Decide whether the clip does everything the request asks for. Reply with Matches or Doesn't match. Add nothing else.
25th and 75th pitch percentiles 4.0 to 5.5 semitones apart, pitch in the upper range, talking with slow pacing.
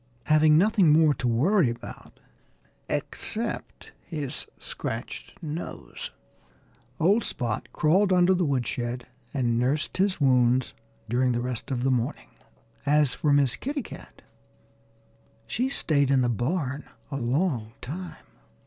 Doesn't match